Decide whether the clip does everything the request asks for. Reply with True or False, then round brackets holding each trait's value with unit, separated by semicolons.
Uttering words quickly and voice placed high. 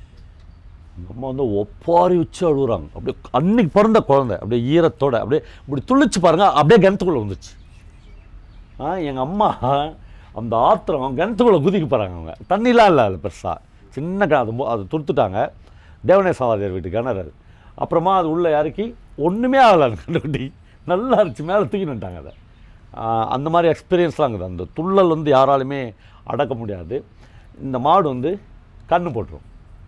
False (135 wpm; 135 Hz)